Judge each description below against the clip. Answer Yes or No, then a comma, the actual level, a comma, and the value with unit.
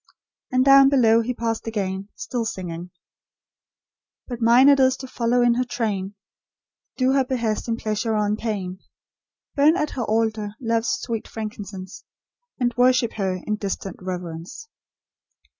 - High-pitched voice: Yes, high, 225 Hz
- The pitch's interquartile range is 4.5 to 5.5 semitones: No, average, 3.5 semitones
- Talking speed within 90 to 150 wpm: Yes, average, 145 wpm